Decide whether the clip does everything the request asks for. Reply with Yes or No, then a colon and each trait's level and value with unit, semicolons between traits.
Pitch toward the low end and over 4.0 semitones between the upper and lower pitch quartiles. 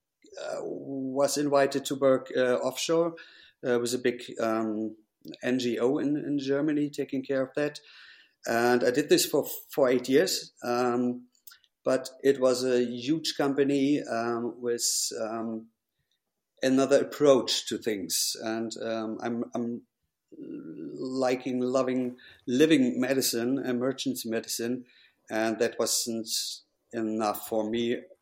No: low, 125 Hz; average, 2.9 semitones